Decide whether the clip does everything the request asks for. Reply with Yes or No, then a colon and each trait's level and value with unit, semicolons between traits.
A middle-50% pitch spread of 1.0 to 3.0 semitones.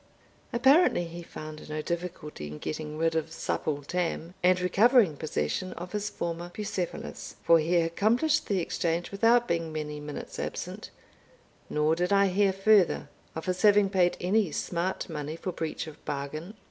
No: average, 3.8 semitones